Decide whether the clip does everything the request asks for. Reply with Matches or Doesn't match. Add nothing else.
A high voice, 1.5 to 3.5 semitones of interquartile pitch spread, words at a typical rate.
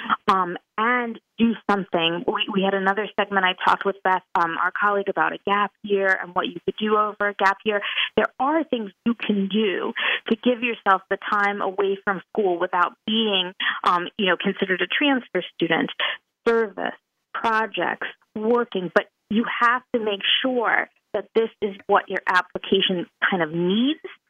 Matches